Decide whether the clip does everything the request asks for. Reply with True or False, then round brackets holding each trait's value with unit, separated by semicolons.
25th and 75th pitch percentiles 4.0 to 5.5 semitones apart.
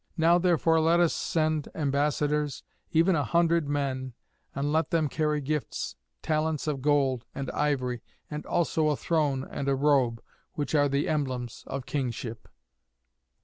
False (2.6 semitones)